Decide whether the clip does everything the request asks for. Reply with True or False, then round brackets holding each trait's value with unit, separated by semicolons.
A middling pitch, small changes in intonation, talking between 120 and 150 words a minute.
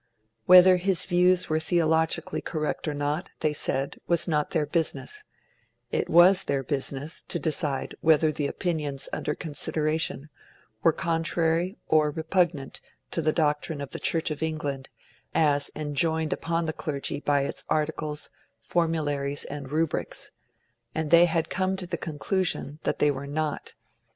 True (155 Hz; 2.3 semitones; 145 wpm)